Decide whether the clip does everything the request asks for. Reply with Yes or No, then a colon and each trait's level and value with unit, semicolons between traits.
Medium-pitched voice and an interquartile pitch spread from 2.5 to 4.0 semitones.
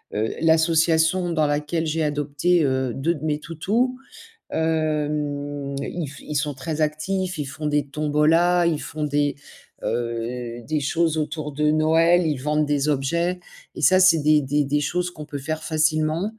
No: medium, 155 Hz; narrow, 2.1 semitones